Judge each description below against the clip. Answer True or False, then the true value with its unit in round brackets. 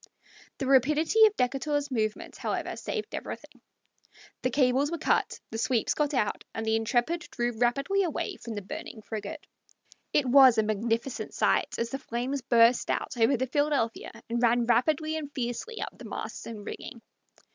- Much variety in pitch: False (4.0 semitones)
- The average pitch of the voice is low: False (250 Hz)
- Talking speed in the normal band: True (170 wpm)